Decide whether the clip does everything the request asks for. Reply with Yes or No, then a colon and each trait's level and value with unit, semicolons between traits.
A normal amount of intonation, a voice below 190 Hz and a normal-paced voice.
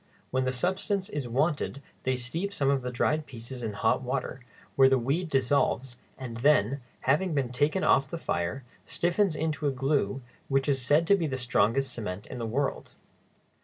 Yes: average, 3.5 semitones; low, 135 Hz; average, 185 wpm